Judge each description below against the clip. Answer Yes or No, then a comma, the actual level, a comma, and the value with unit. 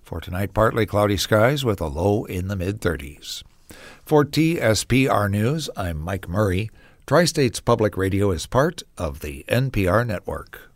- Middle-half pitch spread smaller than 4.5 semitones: No, average, 4.8 semitones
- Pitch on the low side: Yes, low, 105 Hz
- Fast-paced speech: No, average, 155 wpm